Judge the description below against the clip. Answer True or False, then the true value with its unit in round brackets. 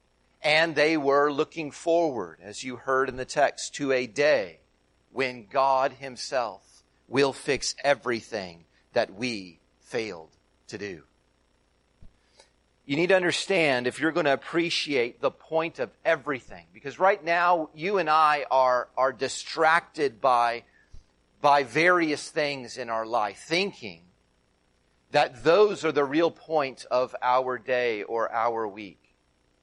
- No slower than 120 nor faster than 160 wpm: True (135 wpm)